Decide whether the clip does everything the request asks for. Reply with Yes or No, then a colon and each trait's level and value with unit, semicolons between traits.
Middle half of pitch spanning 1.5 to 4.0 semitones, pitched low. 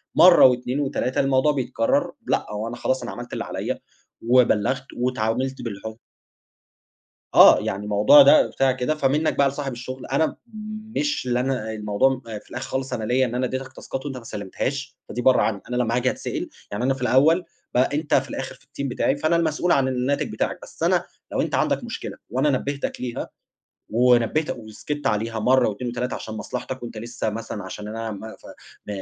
Yes: average, 3.0 semitones; low, 125 Hz